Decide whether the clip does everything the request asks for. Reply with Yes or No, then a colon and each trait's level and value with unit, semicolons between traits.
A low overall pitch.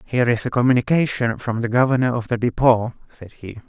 Yes: low, 120 Hz